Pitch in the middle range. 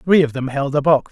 Yes: medium, 145 Hz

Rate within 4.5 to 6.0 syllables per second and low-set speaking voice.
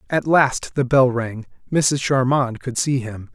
No: 3.8 syllables/s; low, 130 Hz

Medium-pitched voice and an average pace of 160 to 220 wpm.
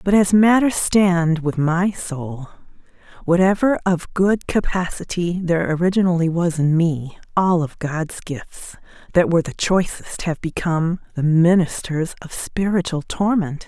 No: medium, 175 Hz; slow, 135 wpm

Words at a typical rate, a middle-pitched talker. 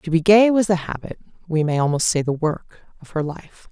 No: fast, 210 wpm; medium, 170 Hz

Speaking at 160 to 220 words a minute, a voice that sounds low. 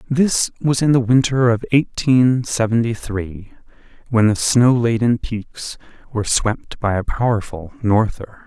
No: average, 140 wpm; low, 115 Hz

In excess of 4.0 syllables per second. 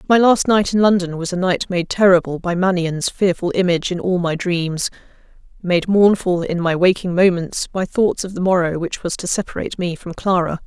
Yes: 5.2 syllables/s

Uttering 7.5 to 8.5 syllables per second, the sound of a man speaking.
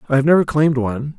Yes: 7.9 syllables/s; male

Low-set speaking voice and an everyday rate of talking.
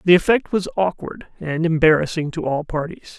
No: medium, 165 Hz; average, 170 wpm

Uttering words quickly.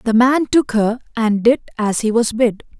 Yes: fast, 215 wpm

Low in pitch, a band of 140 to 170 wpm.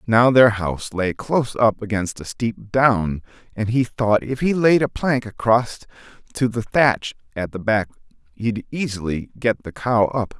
No: low, 115 Hz; average, 180 wpm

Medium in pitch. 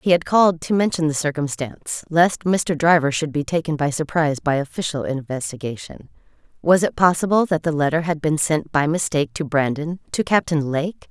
Yes: medium, 155 Hz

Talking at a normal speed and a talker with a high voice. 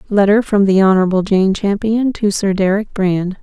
Yes: average, 175 wpm; high, 200 Hz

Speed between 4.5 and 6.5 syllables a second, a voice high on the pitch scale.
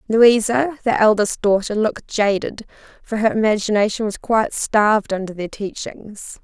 Yes: 4.8 syllables/s; high, 215 Hz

